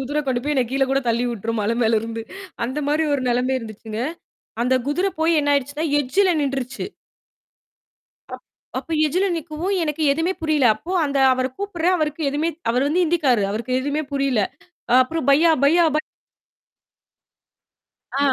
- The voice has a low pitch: No, very high, 280 Hz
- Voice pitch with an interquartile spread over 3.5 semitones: Yes, average, 4.2 semitones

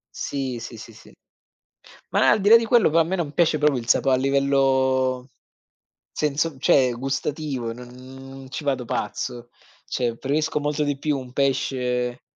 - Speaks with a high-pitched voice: No, low, 135 Hz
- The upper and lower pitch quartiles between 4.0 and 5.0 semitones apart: No, average, 2.8 semitones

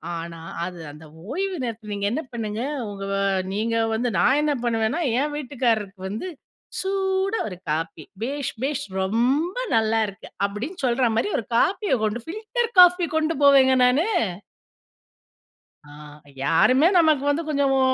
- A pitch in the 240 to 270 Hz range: Yes, very high, 255 Hz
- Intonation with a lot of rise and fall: Yes, wide, 6.7 semitones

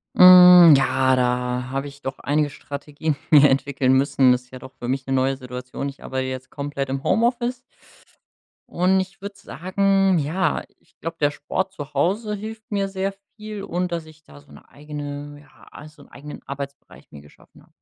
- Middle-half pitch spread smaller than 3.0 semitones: No, wide, 5.4 semitones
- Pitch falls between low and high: Yes, medium, 145 Hz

